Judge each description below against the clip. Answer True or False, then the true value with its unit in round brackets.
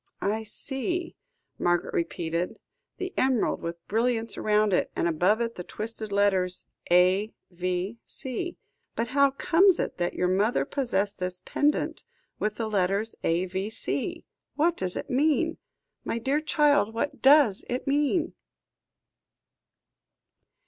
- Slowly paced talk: True (120 wpm)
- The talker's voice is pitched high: True (220 Hz)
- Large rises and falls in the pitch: True (7.2 semitones)